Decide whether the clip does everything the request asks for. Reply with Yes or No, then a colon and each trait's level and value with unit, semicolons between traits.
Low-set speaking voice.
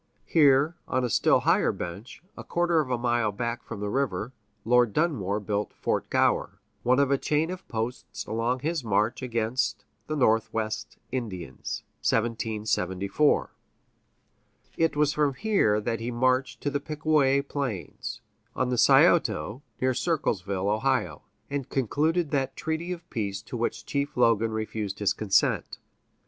Yes: low, 125 Hz